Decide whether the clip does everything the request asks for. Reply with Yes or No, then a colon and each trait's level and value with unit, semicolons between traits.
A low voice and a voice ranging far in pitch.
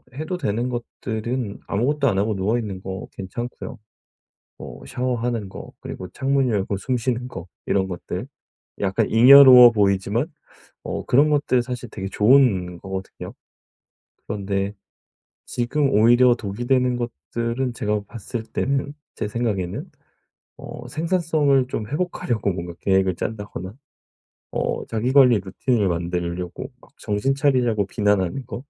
No: low, 115 Hz; average, 4.5 semitones